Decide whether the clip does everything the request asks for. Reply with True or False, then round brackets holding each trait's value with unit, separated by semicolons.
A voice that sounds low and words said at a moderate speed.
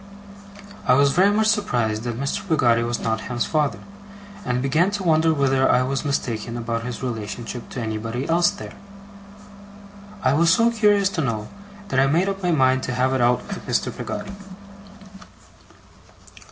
True (130 Hz; 165 wpm)